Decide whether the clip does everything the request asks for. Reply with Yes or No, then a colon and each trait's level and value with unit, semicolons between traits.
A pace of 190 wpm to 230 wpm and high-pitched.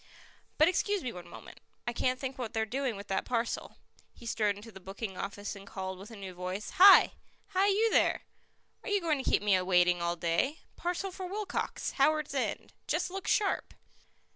Yes: average, 195 wpm; high, 230 Hz